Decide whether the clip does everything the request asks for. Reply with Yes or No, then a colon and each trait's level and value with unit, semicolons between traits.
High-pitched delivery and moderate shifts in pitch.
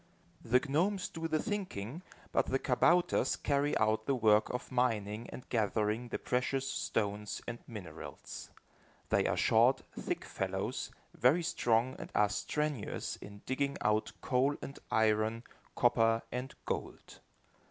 No: low, 125 Hz; average, 4.4 semitones